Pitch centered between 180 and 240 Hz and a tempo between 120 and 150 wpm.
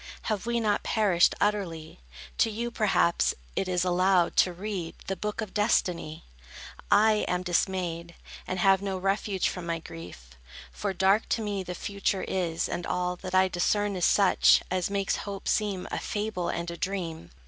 No: high, 190 Hz; average, 170 wpm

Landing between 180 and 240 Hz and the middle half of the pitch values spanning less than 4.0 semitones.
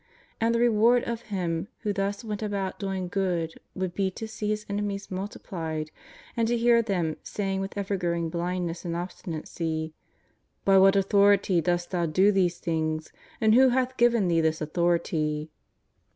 Yes: high, 190 Hz; average, 3.5 semitones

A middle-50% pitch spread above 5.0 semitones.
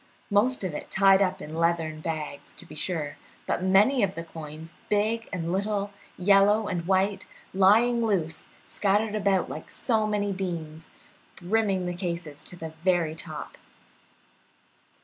No: average, 3.7 semitones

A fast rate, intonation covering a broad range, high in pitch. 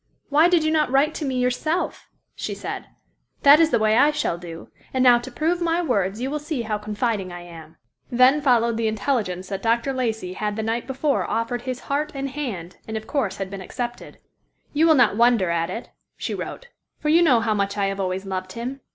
Yes: fast, 220 wpm; wide, 5.8 semitones; high, 240 Hz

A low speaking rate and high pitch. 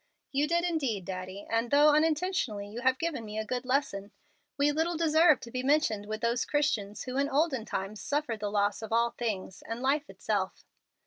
No: average, 195 wpm; very high, 250 Hz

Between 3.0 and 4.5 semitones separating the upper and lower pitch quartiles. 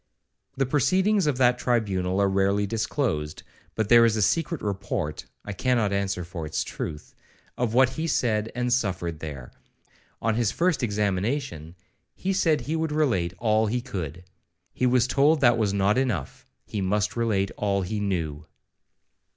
No: average, 5.0 semitones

